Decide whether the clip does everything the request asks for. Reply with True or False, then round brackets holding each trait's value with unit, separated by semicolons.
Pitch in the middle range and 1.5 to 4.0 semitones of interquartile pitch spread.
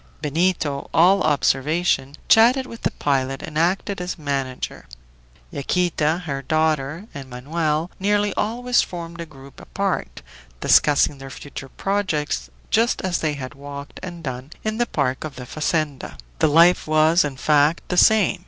False (155 Hz; 4.4 semitones)